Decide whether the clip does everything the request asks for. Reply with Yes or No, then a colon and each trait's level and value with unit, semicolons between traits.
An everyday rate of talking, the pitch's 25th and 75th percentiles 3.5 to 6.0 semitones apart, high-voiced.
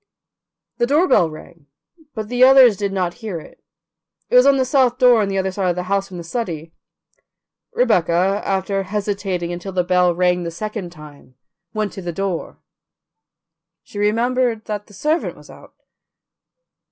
Yes: average, 165 wpm; average, 4.4 semitones; high, 195 Hz